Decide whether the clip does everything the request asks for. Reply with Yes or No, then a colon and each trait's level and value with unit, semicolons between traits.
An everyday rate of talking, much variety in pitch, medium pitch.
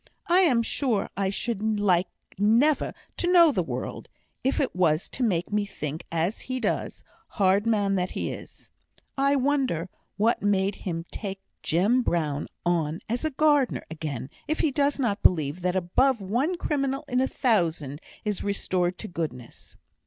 No: average, 160 wpm; wide, 6.9 semitones; high, 205 Hz